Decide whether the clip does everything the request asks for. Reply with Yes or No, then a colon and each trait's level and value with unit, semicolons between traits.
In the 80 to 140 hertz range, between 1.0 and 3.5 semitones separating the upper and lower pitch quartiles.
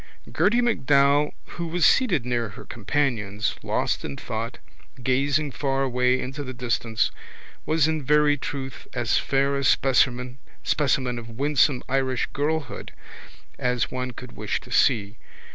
Yes: low, 135 Hz; average, 2.9 semitones